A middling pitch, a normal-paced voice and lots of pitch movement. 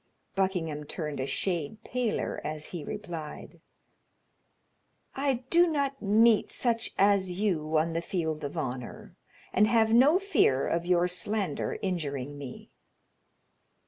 No: medium, 180 Hz; slow, 125 wpm; wide, 6.3 semitones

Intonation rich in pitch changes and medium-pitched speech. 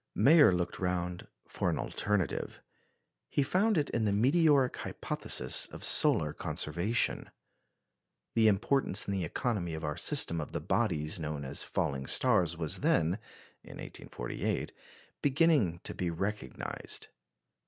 No: wide, 7.3 semitones; very low, 95 Hz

